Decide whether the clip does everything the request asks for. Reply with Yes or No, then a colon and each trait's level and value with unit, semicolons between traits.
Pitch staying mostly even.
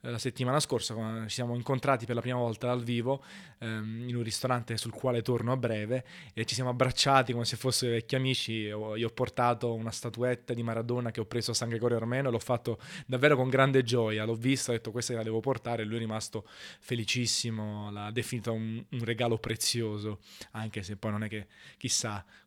Yes: narrow, 2.0 semitones